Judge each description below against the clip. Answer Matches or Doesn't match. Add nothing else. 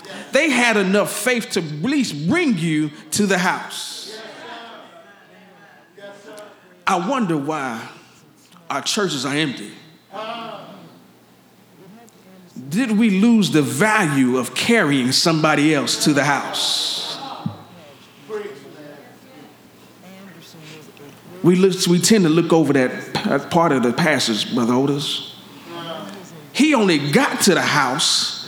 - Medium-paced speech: Doesn't match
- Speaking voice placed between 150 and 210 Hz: Matches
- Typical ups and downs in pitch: Doesn't match